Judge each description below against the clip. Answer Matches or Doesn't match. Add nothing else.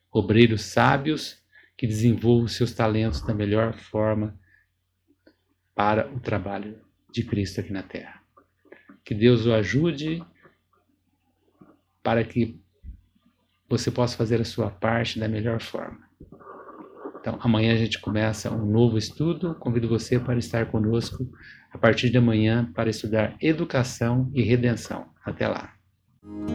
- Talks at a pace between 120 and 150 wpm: Matches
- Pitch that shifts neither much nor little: Doesn't match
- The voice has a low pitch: Matches